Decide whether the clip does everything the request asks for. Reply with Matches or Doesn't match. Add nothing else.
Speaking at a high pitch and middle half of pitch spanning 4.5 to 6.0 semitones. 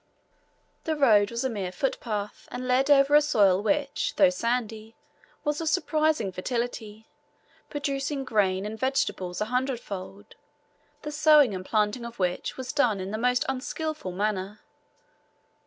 Matches